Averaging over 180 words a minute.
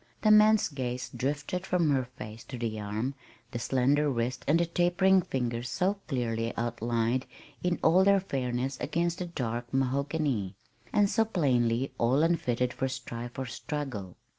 No: average, 155 wpm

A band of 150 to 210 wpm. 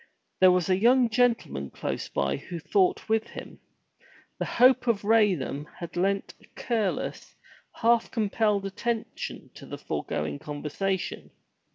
No: slow, 135 wpm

